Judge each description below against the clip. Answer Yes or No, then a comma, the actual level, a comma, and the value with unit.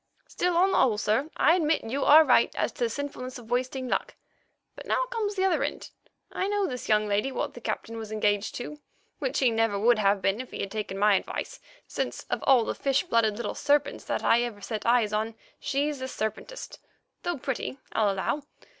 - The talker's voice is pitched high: Yes, high, 245 Hz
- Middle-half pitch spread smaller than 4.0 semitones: No, average, 5.3 semitones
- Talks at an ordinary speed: No, fast, 215 wpm